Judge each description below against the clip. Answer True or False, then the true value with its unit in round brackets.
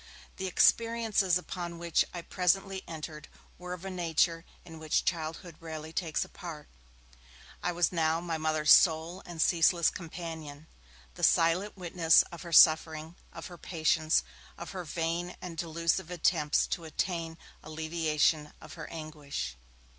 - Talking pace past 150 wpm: False (145 wpm)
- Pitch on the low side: False (165 Hz)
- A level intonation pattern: True (1.9 semitones)